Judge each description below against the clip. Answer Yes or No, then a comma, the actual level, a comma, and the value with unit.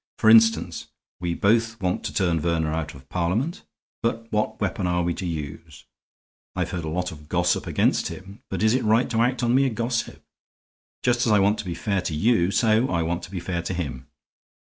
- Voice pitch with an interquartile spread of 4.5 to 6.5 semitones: Yes, average, 5.0 semitones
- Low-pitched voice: Yes, very low, 95 Hz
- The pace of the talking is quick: Yes, fast, 210 wpm